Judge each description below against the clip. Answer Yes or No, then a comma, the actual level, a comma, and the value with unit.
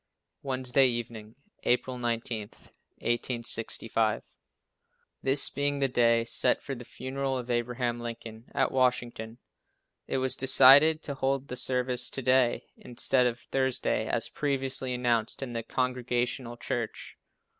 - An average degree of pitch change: No, narrow, 2.0 semitones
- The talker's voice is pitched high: No, low, 125 Hz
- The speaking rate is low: Yes, slow, 125 wpm